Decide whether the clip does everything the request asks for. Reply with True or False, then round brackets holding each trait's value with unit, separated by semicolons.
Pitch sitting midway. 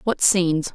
True (180 Hz)